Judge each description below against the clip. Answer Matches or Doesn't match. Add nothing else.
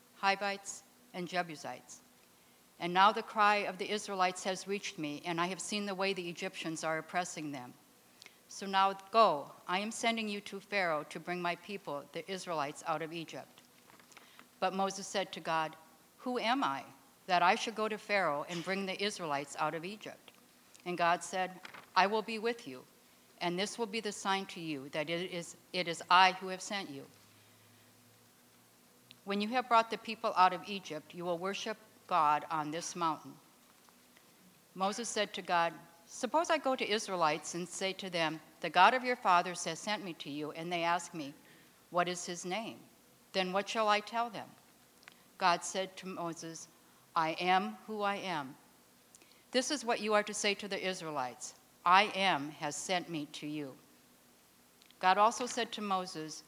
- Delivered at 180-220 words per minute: Matches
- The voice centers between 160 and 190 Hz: Matches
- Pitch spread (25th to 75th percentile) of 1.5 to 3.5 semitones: Doesn't match